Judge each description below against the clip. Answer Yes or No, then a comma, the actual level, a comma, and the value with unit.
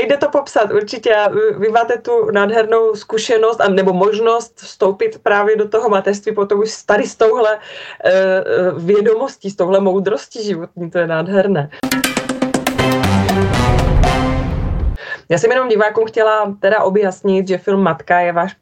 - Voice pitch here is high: Yes, high, 210 Hz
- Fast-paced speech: No, average, 140 wpm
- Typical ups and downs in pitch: Yes, average, 3.0 semitones